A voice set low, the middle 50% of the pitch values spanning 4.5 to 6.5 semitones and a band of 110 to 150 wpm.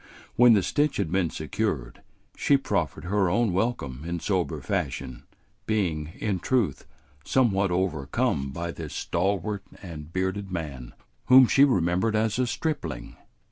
Yes: very low, 95 Hz; wide, 5.6 semitones; average, 140 wpm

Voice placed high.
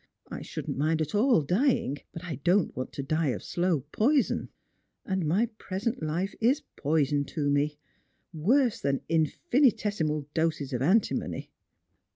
No: medium, 165 Hz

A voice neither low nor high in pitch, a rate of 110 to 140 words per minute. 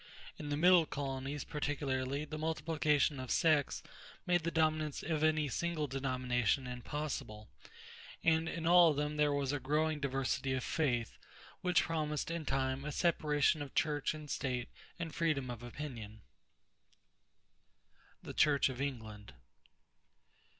Yes: medium, 145 Hz; slow, 135 wpm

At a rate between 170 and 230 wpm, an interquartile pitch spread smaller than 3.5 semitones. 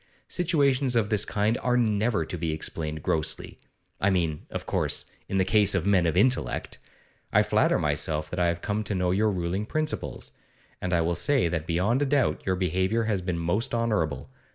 No: average, 195 wpm; average, 4.9 semitones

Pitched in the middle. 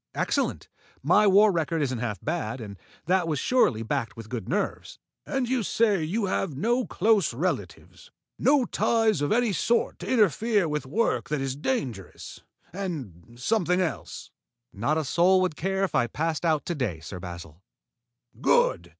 Yes: medium, 165 Hz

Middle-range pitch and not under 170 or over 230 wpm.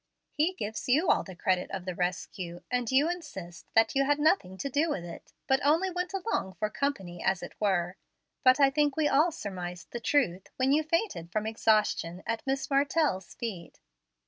No: high, 235 Hz; average, 195 wpm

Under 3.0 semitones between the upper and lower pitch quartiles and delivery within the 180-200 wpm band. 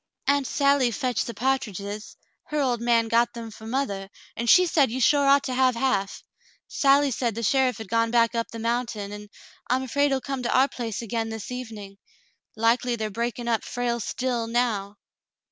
Yes: narrow, 2.6 semitones; average, 195 wpm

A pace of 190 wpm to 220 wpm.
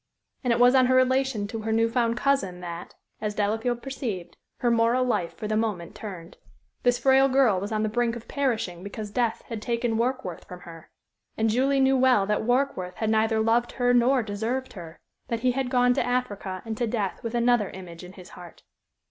Yes: fast, 205 wpm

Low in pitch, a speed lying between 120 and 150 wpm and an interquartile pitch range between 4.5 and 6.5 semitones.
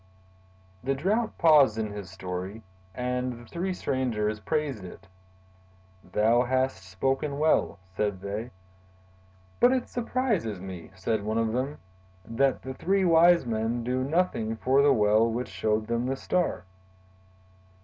Yes: low, 120 Hz; average, 140 wpm; average, 5.2 semitones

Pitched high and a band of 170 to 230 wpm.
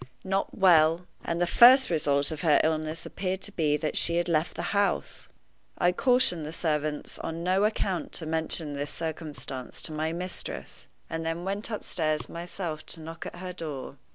No: medium, 165 Hz; average, 180 wpm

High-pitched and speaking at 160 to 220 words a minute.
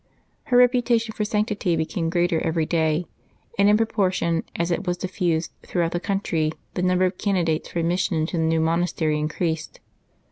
No: medium, 175 Hz; average, 170 wpm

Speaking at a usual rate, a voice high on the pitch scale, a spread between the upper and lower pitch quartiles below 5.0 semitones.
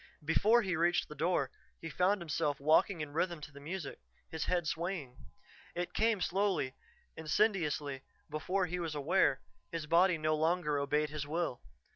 No: average, 160 wpm; medium, 165 Hz; average, 3.3 semitones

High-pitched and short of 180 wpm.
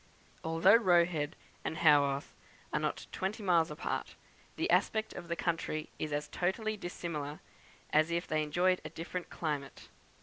No: medium, 170 Hz; average, 155 wpm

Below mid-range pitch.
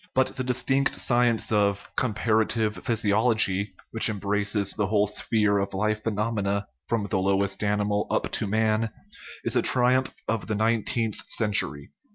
Yes: low, 110 Hz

